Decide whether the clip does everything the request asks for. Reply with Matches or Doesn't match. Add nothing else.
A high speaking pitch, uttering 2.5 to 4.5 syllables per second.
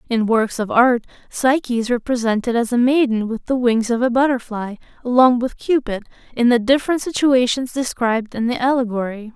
Doesn't match